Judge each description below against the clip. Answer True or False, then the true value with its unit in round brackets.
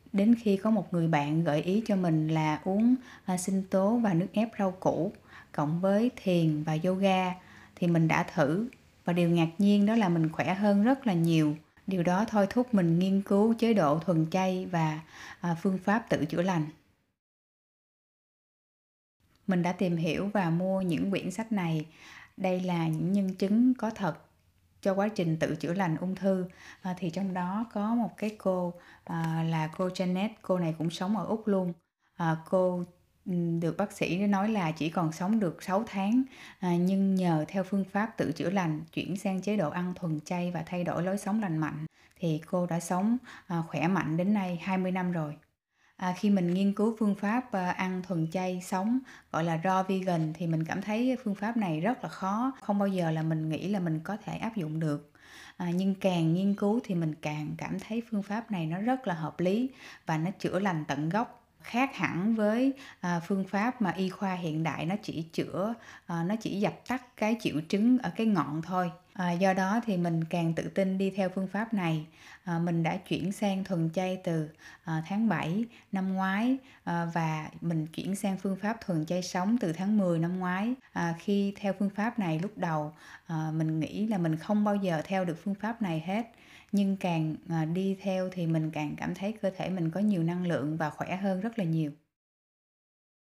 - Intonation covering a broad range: False (3.6 semitones)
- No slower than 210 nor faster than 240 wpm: False (200 wpm)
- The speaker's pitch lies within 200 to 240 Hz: False (185 Hz)